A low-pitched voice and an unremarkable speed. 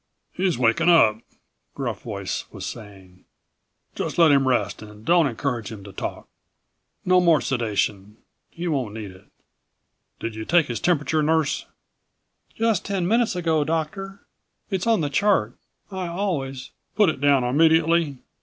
No: medium, 150 Hz; average, 150 wpm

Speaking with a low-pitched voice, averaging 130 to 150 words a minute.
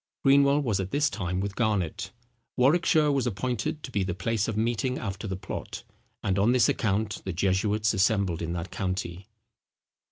No: low, 105 Hz; average, 170 wpm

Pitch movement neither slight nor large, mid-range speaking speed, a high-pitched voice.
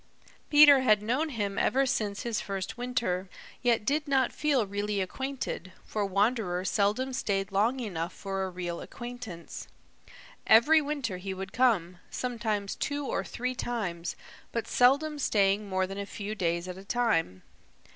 Yes: average, 4.7 semitones; average, 155 wpm; high, 210 Hz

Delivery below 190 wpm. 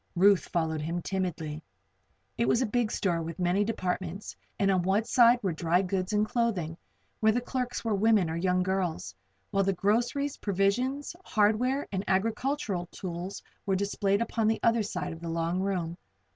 Yes: average, 170 wpm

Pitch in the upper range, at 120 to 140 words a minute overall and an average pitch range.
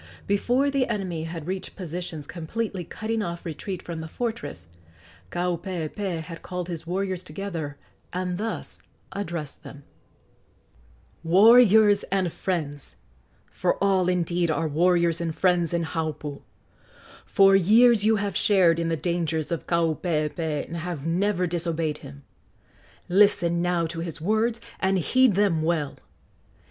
No: medium, 175 Hz; slow, 135 wpm; average, 3.2 semitones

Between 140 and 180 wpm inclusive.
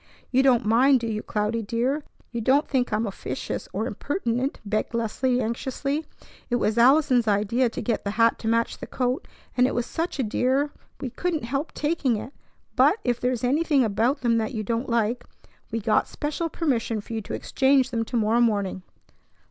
No: average, 190 wpm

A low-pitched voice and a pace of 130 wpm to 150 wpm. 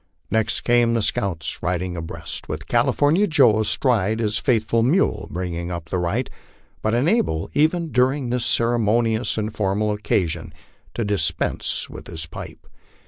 Yes: low, 110 Hz; average, 145 wpm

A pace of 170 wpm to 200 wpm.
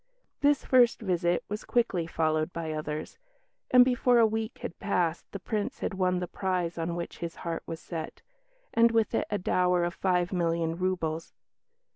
Yes: average, 175 wpm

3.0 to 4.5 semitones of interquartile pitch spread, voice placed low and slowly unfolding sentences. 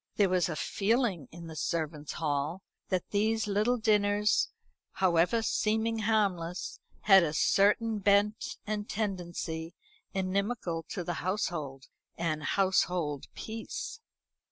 No: average, 4.1 semitones; high, 190 Hz; slow, 115 wpm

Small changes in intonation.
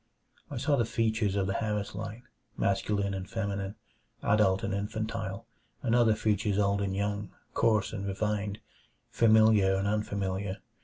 Yes: narrow, 1.8 semitones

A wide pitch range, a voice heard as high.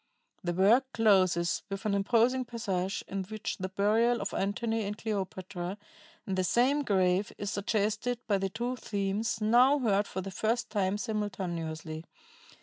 No: average, 3.3 semitones; high, 205 Hz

